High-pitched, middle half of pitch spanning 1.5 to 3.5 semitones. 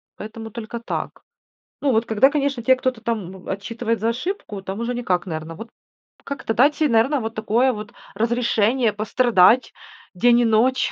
Yes: high, 230 Hz; average, 2.8 semitones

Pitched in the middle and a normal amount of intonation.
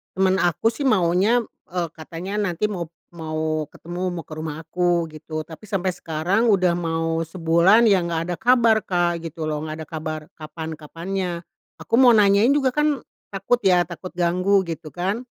Yes: medium, 175 Hz; average, 3.5 semitones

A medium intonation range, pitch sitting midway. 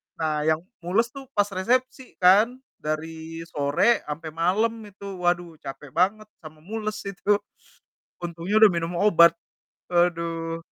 Yes: average, 4.2 semitones; medium, 175 Hz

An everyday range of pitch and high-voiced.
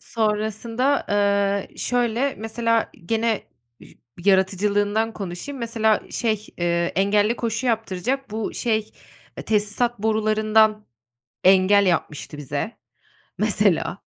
No: narrow, 2.2 semitones; high, 215 Hz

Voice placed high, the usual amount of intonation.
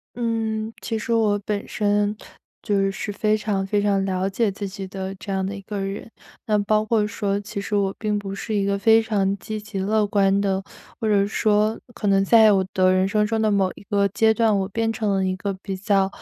No: high, 205 Hz; narrow, 1.7 semitones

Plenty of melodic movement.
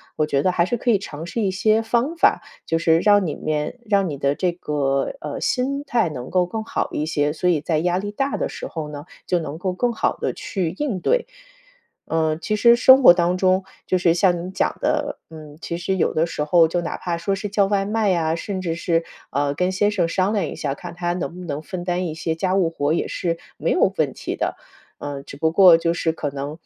No: average, 3.7 semitones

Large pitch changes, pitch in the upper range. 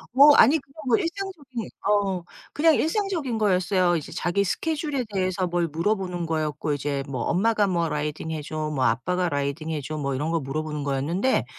No: wide, 7.0 semitones; medium, 175 Hz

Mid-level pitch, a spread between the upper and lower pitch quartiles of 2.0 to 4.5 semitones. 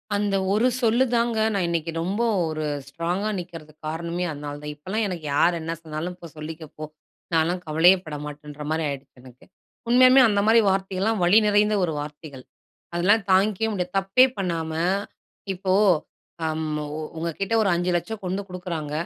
Yes: medium, 175 Hz; average, 4.2 semitones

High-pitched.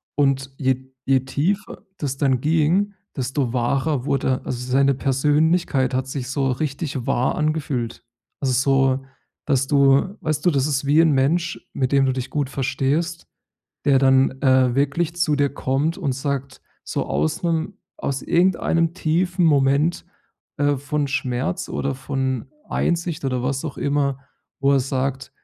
No: medium, 140 Hz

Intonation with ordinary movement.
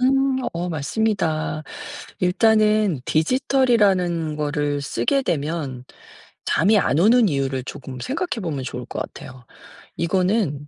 No: wide, 6.9 semitones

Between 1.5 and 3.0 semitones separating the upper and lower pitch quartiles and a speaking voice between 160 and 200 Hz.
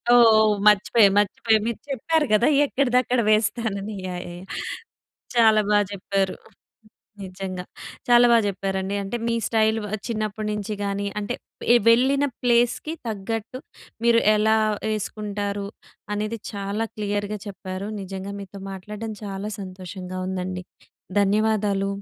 No: narrow, 2.4 semitones; high, 210 Hz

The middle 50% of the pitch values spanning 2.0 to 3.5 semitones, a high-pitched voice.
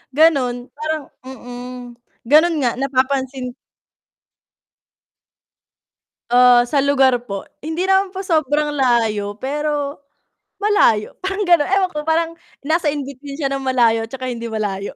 No: average, 4.2 semitones; very high, 275 Hz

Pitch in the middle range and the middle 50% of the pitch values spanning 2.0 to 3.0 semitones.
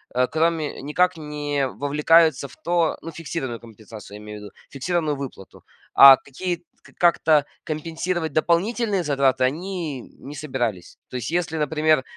No: medium, 150 Hz; average, 3.9 semitones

